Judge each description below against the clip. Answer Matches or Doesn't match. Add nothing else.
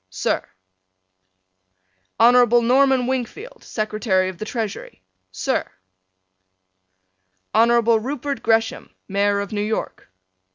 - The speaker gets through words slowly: Matches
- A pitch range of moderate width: Matches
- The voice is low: Doesn't match